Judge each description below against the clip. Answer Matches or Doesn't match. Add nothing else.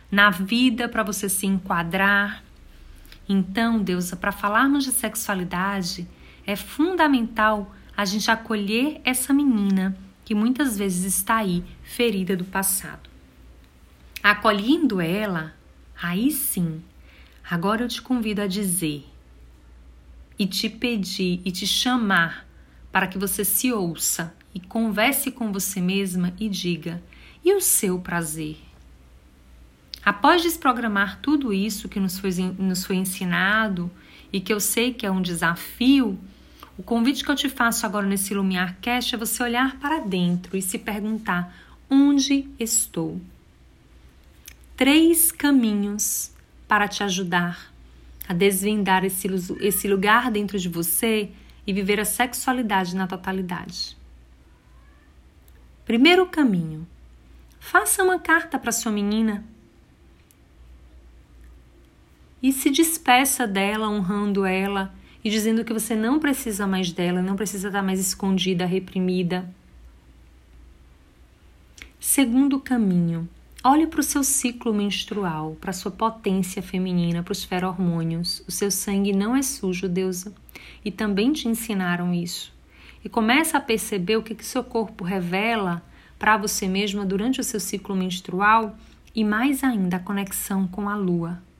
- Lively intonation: Doesn't match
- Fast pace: Doesn't match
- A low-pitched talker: Doesn't match